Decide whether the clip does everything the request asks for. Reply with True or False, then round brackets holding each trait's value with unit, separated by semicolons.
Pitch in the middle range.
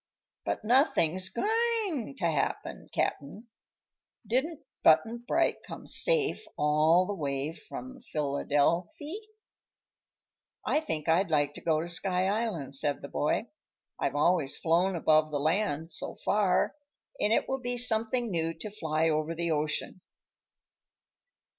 True (175 Hz)